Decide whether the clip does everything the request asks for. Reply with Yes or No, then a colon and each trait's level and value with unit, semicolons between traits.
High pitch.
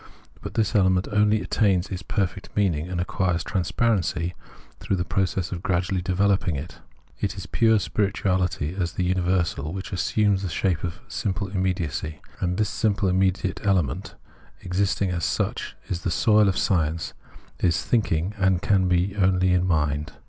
No: very low, 95 Hz